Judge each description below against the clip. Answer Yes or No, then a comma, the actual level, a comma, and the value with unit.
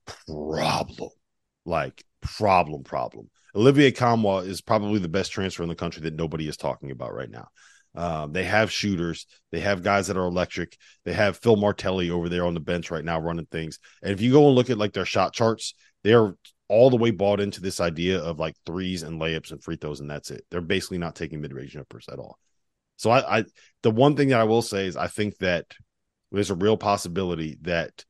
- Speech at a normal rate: No, fast, 220 wpm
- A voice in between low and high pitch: No, very low, 95 Hz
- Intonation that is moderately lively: Yes, average, 4.0 semitones